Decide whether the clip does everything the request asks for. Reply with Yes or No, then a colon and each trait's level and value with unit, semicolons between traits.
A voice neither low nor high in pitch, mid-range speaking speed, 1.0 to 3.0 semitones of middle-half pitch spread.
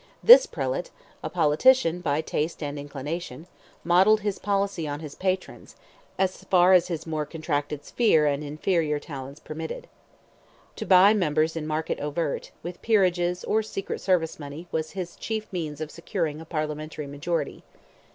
No: medium, 165 Hz; average, 150 wpm; average, 3.6 semitones